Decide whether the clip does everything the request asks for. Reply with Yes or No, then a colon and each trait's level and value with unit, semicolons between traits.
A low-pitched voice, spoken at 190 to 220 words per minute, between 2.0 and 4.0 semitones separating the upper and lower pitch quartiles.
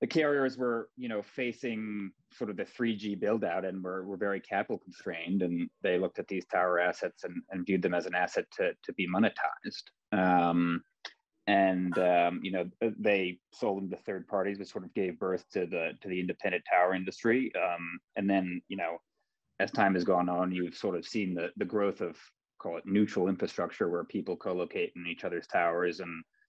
Yes: very low, 95 Hz; average, 200 wpm; average, 2.9 semitones